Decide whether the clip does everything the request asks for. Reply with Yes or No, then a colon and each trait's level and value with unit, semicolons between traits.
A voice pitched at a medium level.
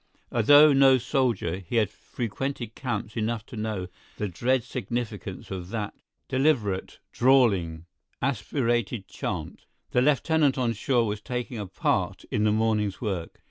No: low, 115 Hz